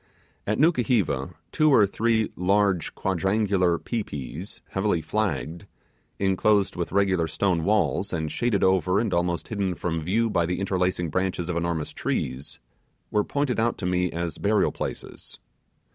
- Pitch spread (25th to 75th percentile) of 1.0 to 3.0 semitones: No, average, 3.5 semitones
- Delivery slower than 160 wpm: Yes, average, 145 wpm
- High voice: No, very low, 95 Hz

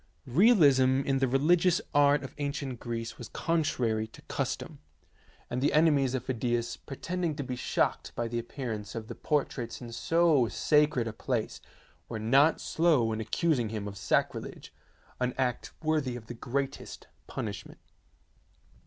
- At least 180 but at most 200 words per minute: No, average, 155 wpm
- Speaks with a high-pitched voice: No, low, 130 Hz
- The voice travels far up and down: No, average, 4.0 semitones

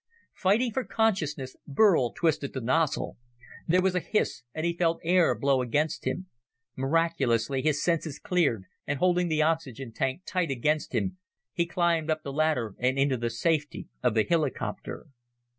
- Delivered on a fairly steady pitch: No, average, 4.3 semitones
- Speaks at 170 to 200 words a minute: No, average, 160 wpm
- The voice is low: No, medium, 155 Hz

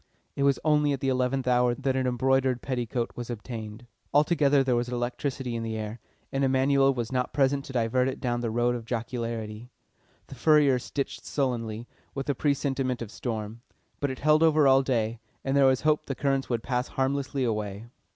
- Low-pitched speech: Yes, low, 130 Hz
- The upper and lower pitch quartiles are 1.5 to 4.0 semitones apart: Yes, narrow, 2.5 semitones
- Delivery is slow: No, average, 190 wpm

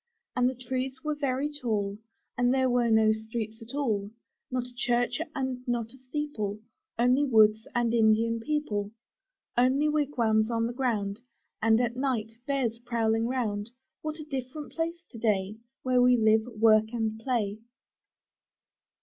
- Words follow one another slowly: No, average, 160 wpm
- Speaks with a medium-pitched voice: No, high, 240 Hz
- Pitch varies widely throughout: No, average, 3.0 semitones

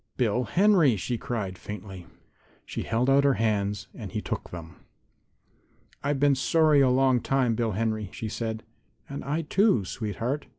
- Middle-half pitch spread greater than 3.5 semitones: Yes, average, 4.6 semitones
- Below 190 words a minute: Yes, average, 160 wpm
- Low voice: Yes, low, 120 Hz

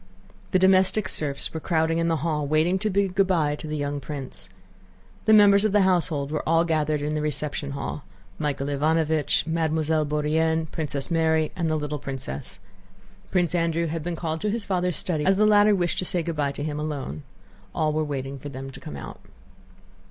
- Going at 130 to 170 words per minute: No, average, 200 wpm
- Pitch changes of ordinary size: Yes, average, 3.0 semitones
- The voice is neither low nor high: Yes, medium, 160 Hz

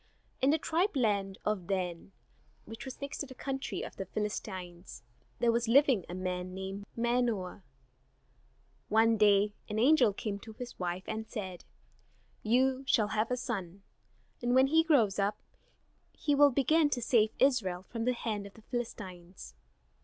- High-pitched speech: Yes, high, 220 Hz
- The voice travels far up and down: No, average, 4.6 semitones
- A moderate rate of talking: Yes, average, 160 wpm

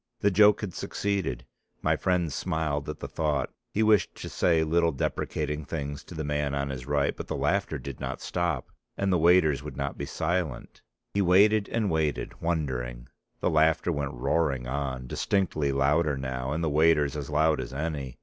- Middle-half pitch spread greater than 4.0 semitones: No, average, 3.7 semitones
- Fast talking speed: No, average, 185 wpm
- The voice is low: Yes, very low, 75 Hz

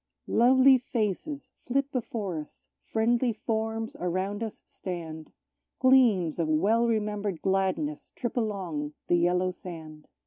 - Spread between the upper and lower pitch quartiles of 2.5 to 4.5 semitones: No, average, 5.2 semitones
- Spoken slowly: Yes, slow, 115 wpm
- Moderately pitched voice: No, high, 210 Hz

